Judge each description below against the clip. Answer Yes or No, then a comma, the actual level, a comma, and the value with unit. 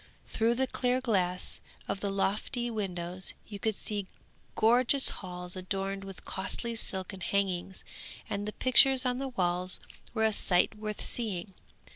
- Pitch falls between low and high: No, high, 200 Hz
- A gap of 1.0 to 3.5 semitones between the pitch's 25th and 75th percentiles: No, average, 3.9 semitones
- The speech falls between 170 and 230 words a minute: No, average, 145 wpm